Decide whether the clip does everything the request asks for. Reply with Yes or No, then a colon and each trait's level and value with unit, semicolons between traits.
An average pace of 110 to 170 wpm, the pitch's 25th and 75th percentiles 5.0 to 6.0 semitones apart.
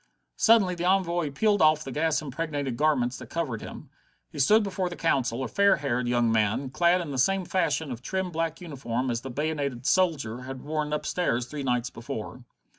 No: average, 190 wpm; wide, 5.5 semitones